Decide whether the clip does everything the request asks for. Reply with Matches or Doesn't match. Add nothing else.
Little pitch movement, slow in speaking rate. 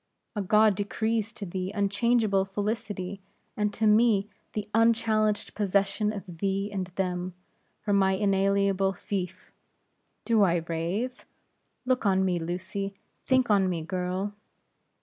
Matches